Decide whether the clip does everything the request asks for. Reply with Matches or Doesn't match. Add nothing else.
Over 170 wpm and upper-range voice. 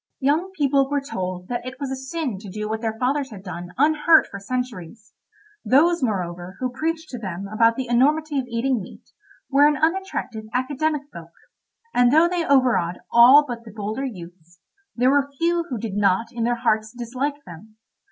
Matches